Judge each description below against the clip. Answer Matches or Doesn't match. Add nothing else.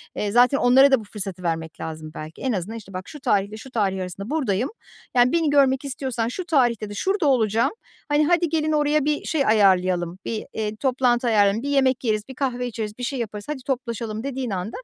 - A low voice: Doesn't match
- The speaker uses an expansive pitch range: Doesn't match